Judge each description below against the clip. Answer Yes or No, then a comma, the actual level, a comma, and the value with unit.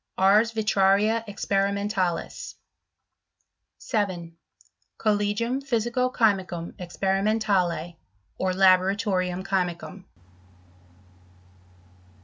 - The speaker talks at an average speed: No, slow, 55 wpm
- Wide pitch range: No, average, 2.7 semitones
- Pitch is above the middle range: Yes, high, 195 Hz